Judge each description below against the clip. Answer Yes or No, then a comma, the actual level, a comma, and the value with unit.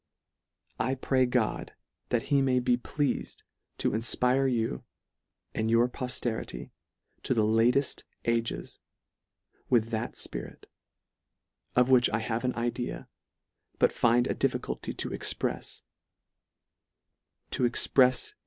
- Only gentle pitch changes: Yes, narrow, 1.9 semitones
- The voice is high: No, low, 120 Hz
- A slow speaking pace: Yes, slow, 125 wpm